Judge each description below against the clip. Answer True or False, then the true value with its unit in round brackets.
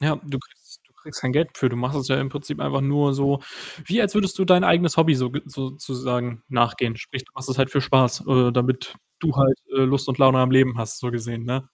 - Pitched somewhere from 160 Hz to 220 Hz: False (135 Hz)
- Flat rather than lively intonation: True (2.2 semitones)